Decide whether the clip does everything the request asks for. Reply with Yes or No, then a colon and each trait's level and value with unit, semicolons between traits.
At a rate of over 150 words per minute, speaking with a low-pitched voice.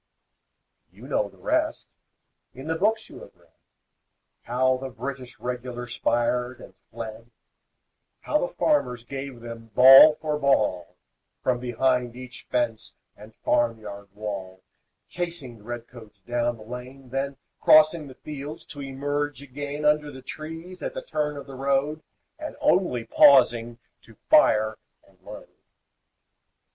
No: average, 140 wpm; low, 130 Hz